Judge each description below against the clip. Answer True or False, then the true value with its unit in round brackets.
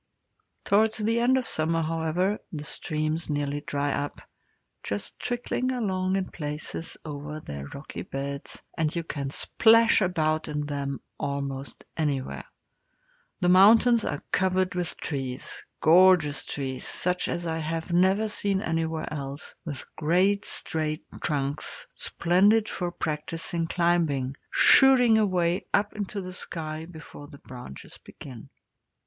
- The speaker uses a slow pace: True (130 wpm)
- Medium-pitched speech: True (165 Hz)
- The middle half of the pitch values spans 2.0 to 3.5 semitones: False (4.3 semitones)